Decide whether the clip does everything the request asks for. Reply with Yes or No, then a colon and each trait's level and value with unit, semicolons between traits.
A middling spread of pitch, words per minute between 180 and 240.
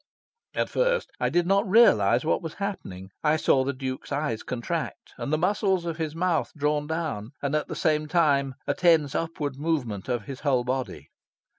Yes: average, 4.3 semitones; average, 185 wpm